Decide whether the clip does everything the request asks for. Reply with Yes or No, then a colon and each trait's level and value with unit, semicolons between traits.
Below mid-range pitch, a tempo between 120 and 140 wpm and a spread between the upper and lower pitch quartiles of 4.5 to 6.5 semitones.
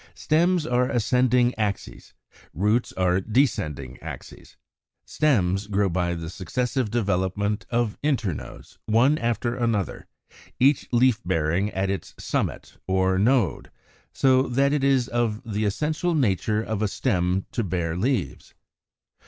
Yes: low, 110 Hz; slow, 135 wpm; average, 5.0 semitones